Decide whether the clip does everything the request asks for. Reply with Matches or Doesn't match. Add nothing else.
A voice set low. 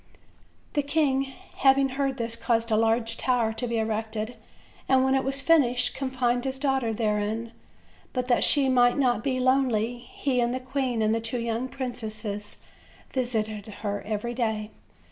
Doesn't match